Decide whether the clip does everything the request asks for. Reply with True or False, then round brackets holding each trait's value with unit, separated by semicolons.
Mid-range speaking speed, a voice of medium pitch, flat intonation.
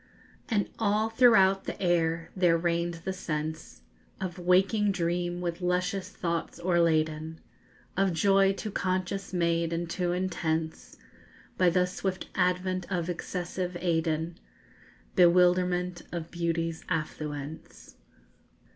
False (110 wpm; 175 Hz; 1.9 semitones)